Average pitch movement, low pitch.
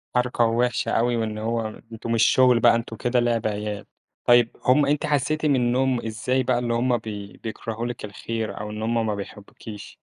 No: narrow, 2.1 semitones; low, 115 Hz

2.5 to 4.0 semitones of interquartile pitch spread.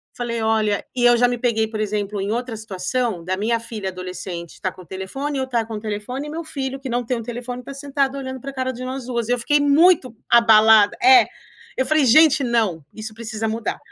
Yes: average, 3.5 semitones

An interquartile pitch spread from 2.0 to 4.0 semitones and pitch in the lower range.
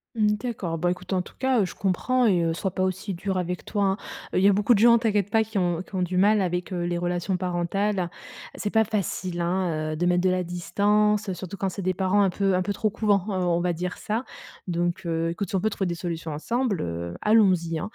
No: average, 2.9 semitones; medium, 185 Hz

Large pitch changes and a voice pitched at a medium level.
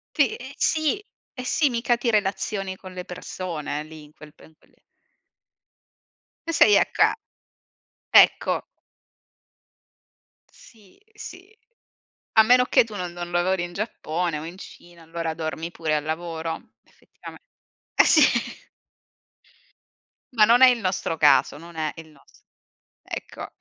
Yes: wide, 5.9 semitones; medium, 180 Hz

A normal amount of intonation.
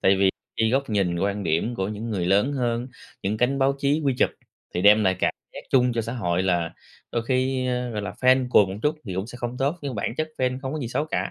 Yes: average, 4.6 semitones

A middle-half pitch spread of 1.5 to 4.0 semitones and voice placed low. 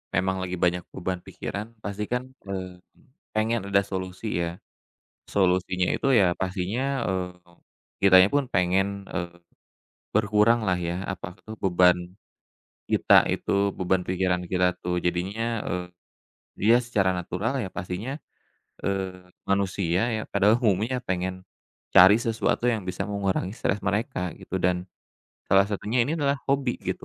Yes: narrow, 2.5 semitones; very low, 95 Hz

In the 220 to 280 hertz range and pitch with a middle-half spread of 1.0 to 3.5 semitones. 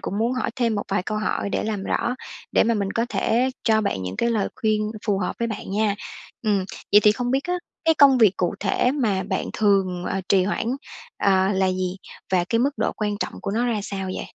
No: high, 210 Hz; average, 3.2 semitones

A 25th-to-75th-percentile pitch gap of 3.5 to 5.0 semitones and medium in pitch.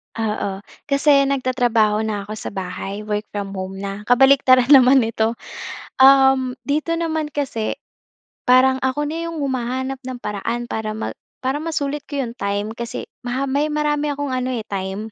No: average, 4.4 semitones; very high, 255 Hz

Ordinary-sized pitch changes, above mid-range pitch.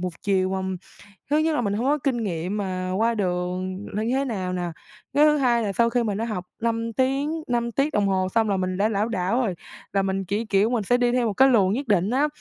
Yes: average, 4.4 semitones; high, 215 Hz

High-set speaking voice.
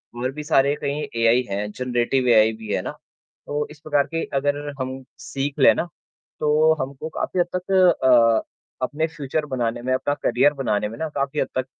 No: low, 135 Hz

